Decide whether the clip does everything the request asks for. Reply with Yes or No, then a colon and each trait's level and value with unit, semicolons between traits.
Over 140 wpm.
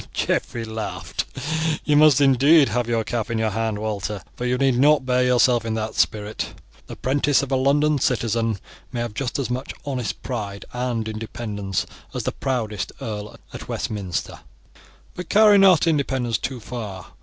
Yes: average, 165 wpm